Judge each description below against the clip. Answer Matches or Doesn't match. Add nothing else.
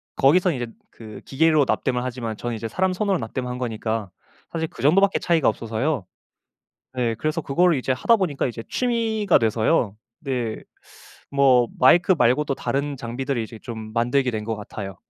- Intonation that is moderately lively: Doesn't match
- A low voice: Matches